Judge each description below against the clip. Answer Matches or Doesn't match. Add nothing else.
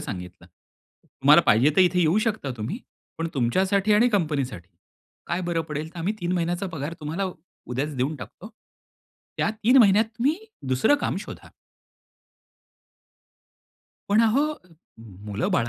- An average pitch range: Doesn't match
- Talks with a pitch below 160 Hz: Doesn't match